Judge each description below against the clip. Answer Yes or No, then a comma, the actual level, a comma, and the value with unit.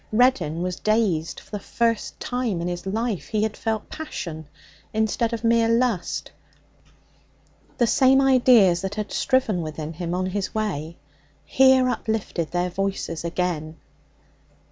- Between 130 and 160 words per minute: Yes, average, 140 wpm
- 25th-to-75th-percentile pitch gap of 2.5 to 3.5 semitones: No, average, 4.9 semitones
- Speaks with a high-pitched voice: Yes, high, 210 Hz